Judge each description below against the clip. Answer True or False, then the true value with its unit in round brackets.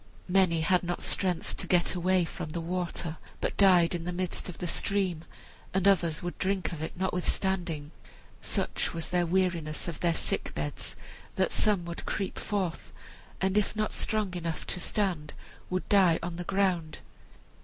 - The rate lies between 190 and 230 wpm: False (170 wpm)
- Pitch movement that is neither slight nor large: False (2.1 semitones)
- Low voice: False (180 Hz)